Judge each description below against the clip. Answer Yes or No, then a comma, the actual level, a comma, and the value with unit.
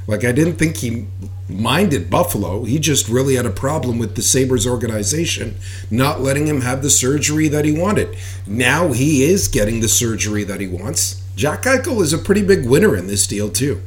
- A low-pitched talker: Yes, low, 120 Hz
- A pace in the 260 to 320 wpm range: No, average, 200 wpm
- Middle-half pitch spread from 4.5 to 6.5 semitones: Yes, wide, 5.4 semitones